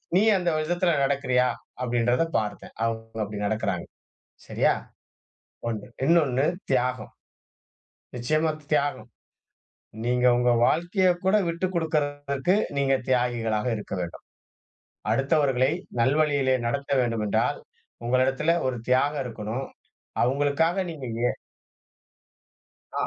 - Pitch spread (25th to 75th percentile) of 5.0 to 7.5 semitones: No, average, 4.2 semitones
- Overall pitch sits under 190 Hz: Yes, low, 135 Hz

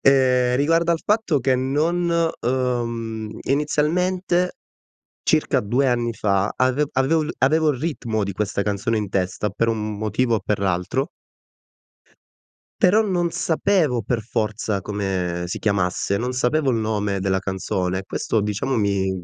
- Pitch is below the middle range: Yes, low, 120 Hz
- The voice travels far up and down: Yes, wide, 6.4 semitones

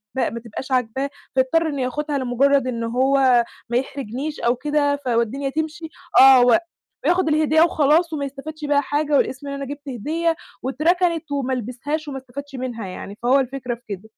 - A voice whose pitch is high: Yes, very high, 275 Hz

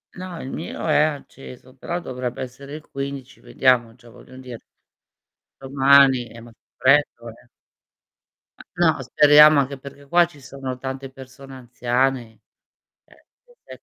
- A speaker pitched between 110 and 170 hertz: Yes, low, 135 Hz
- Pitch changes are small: Yes, narrow, 2.1 semitones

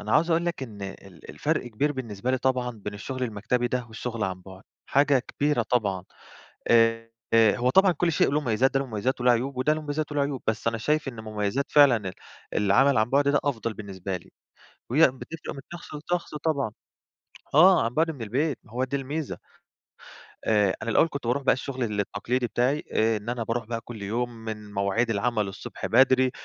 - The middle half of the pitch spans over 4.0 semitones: Yes, average, 4.4 semitones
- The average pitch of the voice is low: Yes, low, 120 Hz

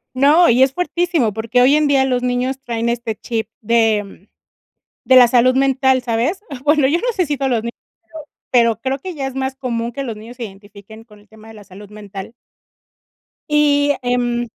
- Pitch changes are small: No, average, 3.4 semitones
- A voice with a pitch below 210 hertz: No, high, 245 Hz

